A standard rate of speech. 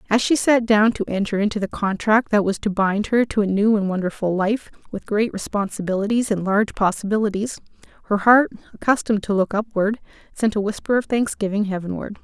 Yes: average, 185 wpm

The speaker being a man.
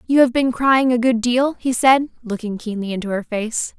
No: female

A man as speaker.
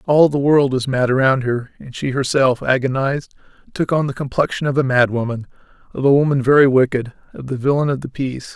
Yes: male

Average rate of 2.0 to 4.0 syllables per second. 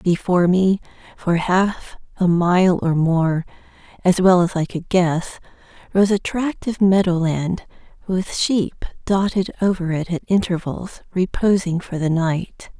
Yes: 3.7 syllables/s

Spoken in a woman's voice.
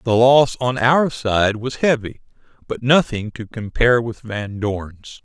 No: male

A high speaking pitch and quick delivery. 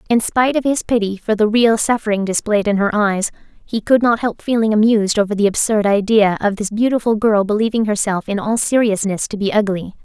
Yes: high, 215 Hz; fast, 210 wpm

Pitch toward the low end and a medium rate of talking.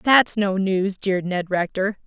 No: high, 195 Hz; average, 175 wpm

